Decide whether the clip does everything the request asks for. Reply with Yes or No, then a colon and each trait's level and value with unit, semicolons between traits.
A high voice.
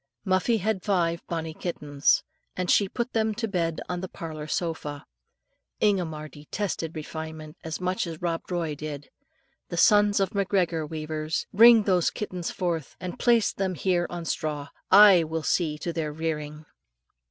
No: medium, 170 Hz